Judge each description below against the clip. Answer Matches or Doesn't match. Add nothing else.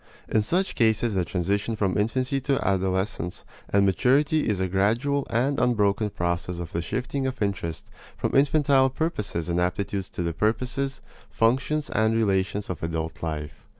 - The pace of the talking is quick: Doesn't match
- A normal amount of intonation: Doesn't match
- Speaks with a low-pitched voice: Matches